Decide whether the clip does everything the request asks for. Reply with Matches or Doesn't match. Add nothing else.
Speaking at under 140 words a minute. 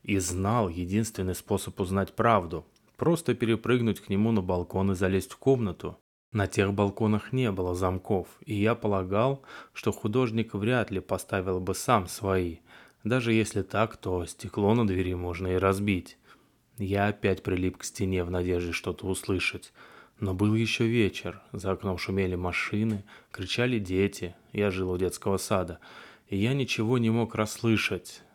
Doesn't match